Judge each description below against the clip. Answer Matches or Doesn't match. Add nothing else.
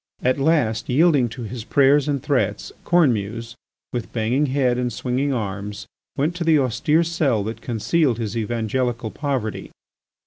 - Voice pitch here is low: Matches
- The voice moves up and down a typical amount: Matches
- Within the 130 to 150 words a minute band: Matches